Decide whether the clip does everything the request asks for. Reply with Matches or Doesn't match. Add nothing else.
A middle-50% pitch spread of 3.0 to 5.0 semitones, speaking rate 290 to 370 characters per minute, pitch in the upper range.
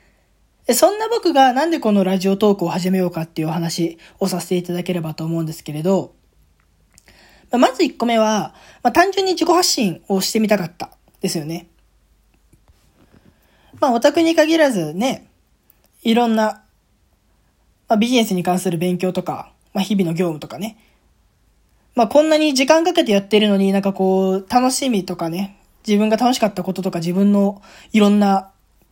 Doesn't match